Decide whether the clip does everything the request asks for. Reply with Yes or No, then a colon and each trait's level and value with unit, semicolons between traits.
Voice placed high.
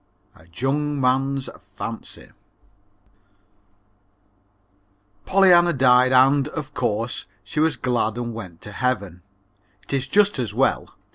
No: low, 130 Hz